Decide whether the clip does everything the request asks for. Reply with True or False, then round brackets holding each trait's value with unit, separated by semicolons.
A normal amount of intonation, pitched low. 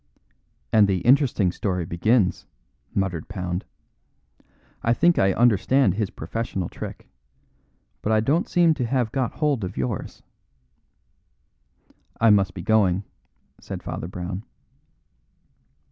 True (4.9 semitones; 105 Hz)